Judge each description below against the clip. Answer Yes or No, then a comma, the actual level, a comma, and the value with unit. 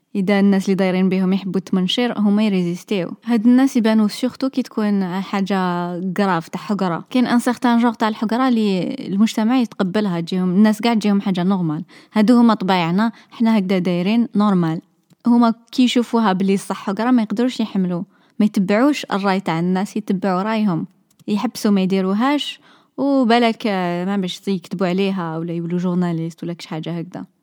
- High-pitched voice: Yes, high, 200 Hz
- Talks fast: Yes, fast, 160 wpm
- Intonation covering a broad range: No, average, 3.7 semitones